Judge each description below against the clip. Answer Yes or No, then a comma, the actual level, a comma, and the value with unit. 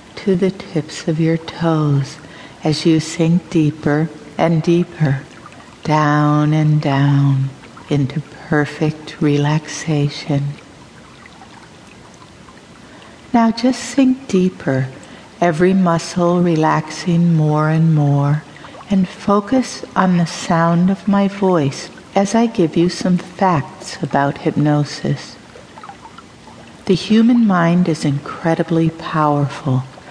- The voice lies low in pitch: No, medium, 160 Hz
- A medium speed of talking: No, slow, 100 wpm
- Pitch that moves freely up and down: No, average, 3.5 semitones